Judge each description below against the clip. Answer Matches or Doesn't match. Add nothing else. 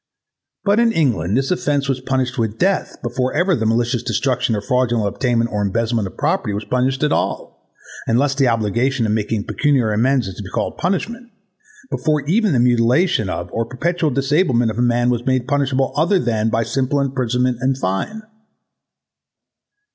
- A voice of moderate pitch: Doesn't match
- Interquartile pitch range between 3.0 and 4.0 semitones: Matches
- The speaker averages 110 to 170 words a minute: Doesn't match